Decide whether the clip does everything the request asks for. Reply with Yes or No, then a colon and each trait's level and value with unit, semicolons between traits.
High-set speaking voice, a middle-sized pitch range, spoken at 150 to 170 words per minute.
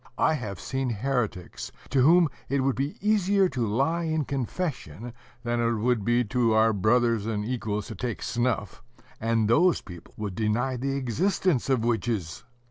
No: low, 120 Hz; average, 3.9 semitones; average, 160 wpm